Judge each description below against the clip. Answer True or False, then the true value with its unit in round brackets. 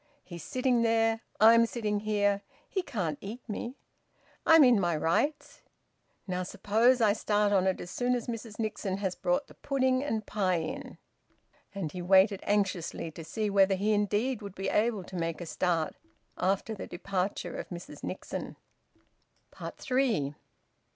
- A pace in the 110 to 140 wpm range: False (155 wpm)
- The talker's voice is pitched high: True (205 Hz)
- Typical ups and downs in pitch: True (3.9 semitones)